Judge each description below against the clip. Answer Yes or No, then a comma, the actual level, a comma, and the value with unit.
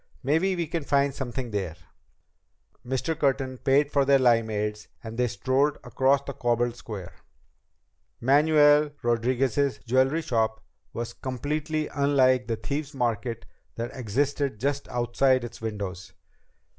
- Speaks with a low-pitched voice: Yes, low, 130 Hz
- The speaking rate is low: Yes, slow, 125 wpm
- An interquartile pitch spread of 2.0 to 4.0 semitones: Yes, average, 3.4 semitones